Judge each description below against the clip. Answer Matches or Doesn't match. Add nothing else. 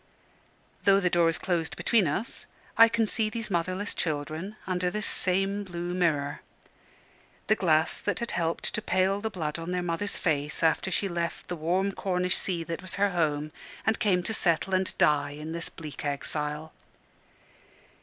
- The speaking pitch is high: Doesn't match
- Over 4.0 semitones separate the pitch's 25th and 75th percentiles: Doesn't match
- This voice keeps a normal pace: Matches